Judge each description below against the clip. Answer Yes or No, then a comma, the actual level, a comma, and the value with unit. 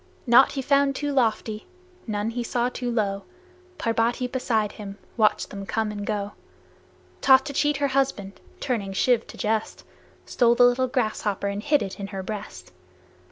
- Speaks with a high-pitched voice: Yes, high, 230 Hz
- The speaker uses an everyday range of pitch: Yes, average, 3.8 semitones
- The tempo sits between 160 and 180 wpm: Yes, average, 165 wpm